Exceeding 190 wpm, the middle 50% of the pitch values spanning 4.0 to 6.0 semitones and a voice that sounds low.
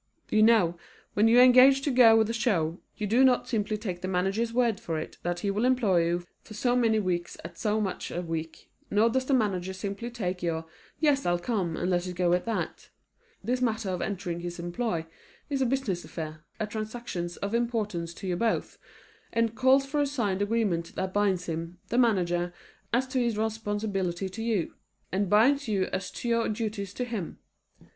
No: average, 200 wpm; average, 4.7 semitones; high, 210 Hz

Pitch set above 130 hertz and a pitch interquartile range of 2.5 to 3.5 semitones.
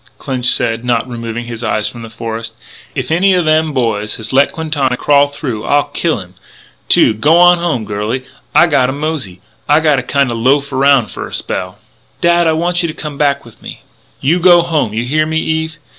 No: medium, 140 Hz; average, 5.3 semitones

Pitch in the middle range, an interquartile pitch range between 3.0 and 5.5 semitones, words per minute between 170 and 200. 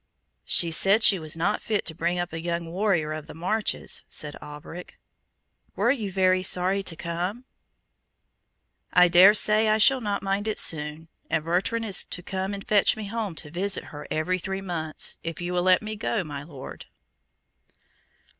Yes: medium, 180 Hz; average, 3.7 semitones; average, 180 wpm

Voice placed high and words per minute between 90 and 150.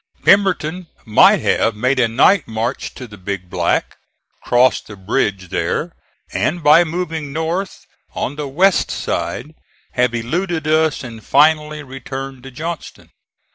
No: low, 135 Hz; slow, 135 wpm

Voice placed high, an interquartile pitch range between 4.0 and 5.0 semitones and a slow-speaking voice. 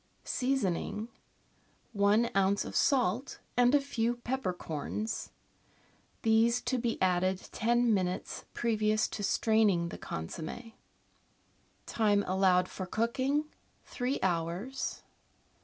Yes: high, 220 Hz; average, 4.3 semitones; slow, 105 wpm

